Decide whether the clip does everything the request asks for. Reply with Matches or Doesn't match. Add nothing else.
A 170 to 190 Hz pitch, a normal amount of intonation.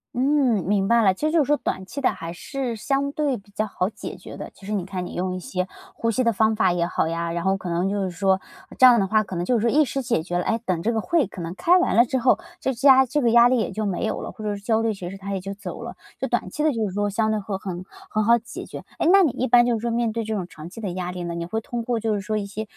Doesn't match